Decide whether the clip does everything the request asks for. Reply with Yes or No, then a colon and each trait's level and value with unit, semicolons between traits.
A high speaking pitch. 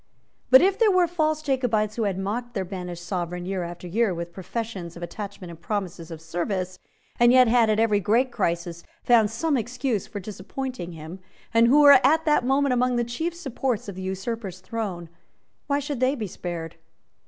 Yes: high, 215 Hz